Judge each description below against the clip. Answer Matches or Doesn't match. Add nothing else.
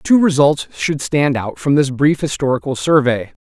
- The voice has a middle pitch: Matches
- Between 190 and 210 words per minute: Doesn't match